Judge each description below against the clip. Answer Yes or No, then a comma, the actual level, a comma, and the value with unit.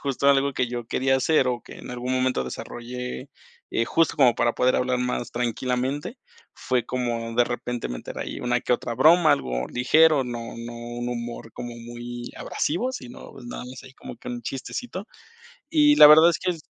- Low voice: Yes, low, 125 Hz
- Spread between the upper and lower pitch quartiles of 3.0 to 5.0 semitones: No, narrow, 2.6 semitones